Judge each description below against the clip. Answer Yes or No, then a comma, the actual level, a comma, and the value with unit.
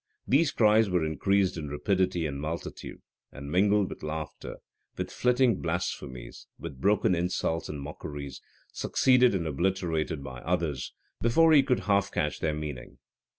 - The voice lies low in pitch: Yes, very low, 85 Hz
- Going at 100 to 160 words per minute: Yes, average, 145 wpm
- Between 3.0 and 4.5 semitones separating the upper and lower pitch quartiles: No, average, 5.1 semitones